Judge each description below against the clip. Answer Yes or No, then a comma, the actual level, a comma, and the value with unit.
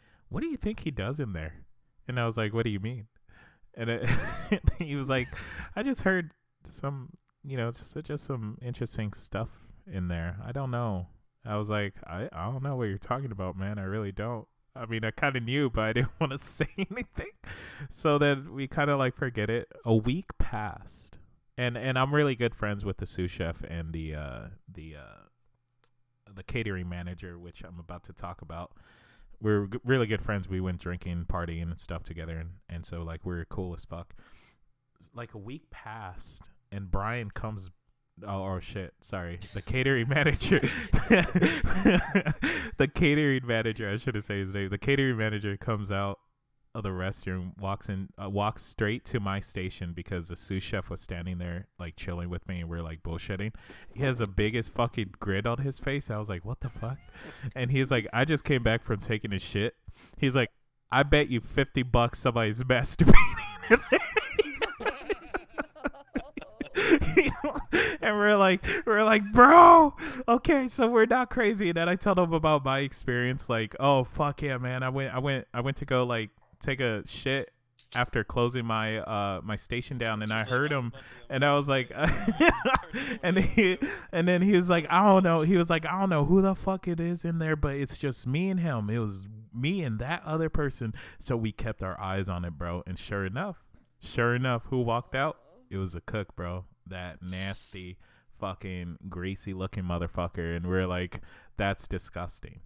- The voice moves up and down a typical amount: No, wide, 6.3 semitones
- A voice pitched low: Yes, low, 115 Hz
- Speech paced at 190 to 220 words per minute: Yes, average, 195 wpm